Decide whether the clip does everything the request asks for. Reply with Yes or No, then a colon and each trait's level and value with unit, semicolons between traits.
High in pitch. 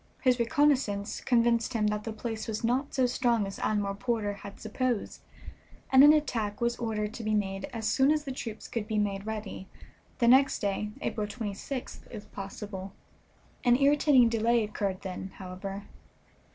Yes: high, 220 Hz